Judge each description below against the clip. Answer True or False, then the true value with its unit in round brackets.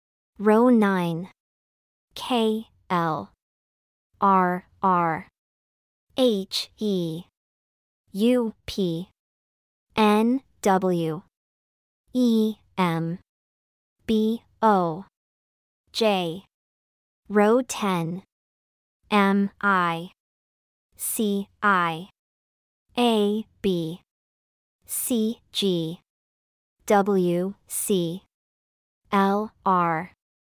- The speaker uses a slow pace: True (60 wpm)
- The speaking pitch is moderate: True (180 Hz)